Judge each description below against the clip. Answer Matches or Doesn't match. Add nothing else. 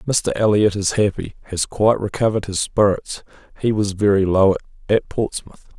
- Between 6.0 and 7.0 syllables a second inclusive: Doesn't match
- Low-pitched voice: Matches